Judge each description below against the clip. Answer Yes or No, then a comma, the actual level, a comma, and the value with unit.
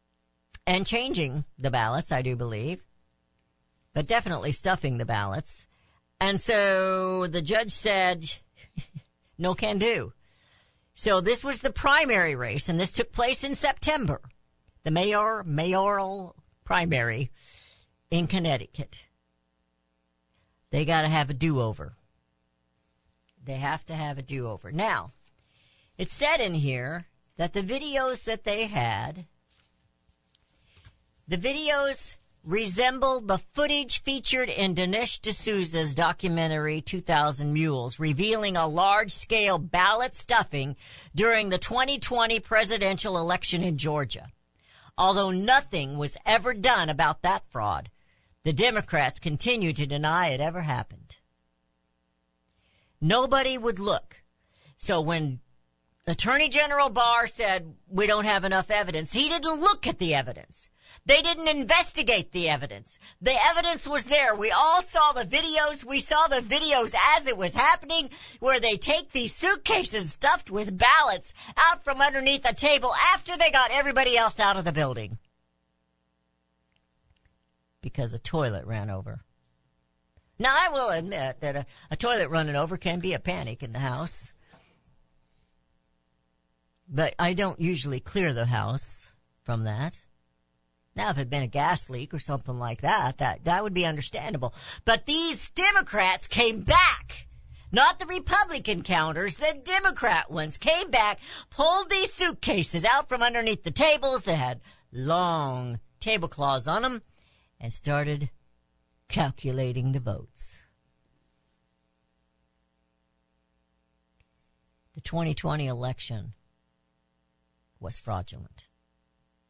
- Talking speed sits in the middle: No, slow, 130 wpm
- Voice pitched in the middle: Yes, medium, 165 Hz